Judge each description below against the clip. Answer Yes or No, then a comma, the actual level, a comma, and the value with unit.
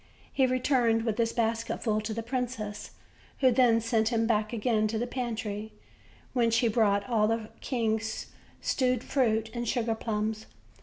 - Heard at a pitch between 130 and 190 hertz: No, high, 225 Hz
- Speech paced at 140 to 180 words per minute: Yes, average, 155 wpm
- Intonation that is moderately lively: No, narrow, 1.8 semitones